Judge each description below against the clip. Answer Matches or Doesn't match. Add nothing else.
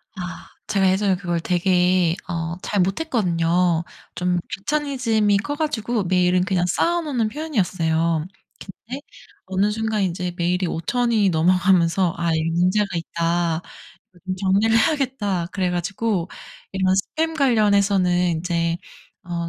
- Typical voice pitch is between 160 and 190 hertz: Matches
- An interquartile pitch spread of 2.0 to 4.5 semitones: Matches